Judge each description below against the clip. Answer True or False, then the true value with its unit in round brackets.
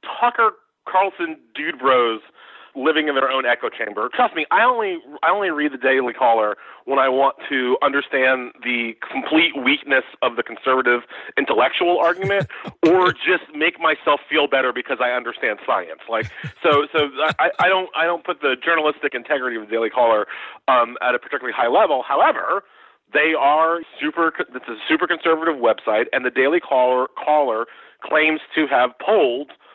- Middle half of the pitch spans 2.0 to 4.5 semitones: False (5.2 semitones)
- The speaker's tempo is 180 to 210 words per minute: False (165 wpm)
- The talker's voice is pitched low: False (155 Hz)